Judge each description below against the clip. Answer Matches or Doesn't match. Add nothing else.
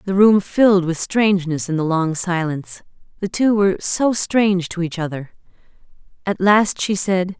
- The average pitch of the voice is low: Doesn't match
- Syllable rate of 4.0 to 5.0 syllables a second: Matches